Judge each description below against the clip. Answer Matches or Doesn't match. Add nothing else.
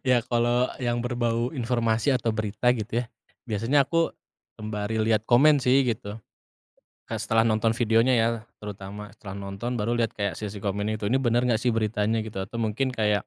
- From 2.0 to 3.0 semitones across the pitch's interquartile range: Matches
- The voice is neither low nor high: Doesn't match